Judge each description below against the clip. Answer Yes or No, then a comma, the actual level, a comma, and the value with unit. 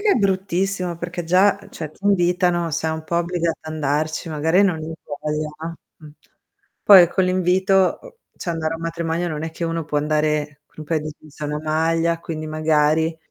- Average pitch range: No, narrow, 2.2 semitones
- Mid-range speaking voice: Yes, medium, 165 Hz